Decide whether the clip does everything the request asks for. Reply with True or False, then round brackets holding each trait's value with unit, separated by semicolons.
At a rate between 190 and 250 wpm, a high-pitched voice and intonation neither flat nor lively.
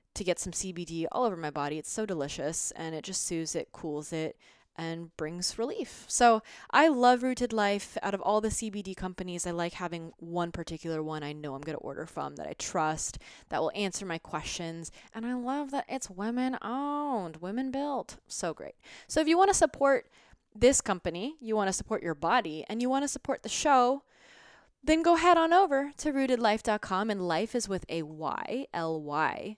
False (205 wpm; 200 Hz; 7.4 semitones)